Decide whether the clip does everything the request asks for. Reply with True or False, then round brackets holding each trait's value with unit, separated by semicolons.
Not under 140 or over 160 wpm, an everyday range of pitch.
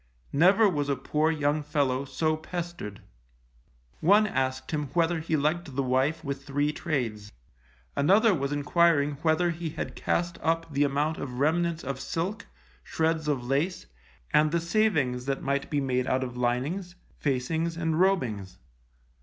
True (155 wpm; 3.7 semitones)